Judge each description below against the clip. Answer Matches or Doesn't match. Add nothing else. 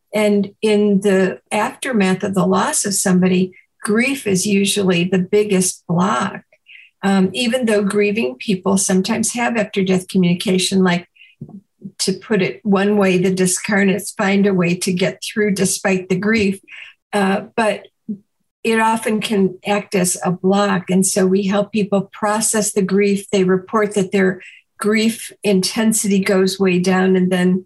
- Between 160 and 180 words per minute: Doesn't match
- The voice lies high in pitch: Matches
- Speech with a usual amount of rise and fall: Doesn't match